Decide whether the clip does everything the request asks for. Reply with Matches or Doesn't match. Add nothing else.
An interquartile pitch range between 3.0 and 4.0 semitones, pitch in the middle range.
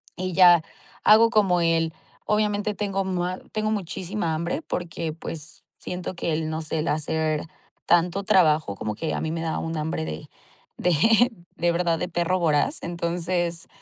Doesn't match